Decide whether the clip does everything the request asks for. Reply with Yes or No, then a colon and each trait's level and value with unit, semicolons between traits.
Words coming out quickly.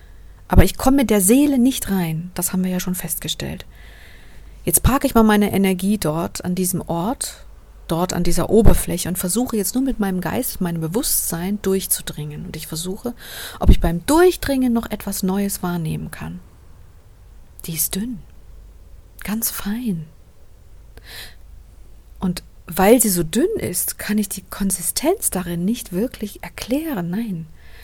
No: average, 150 wpm